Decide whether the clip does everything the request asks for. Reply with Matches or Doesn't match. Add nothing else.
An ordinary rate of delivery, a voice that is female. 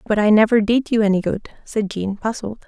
Doesn't match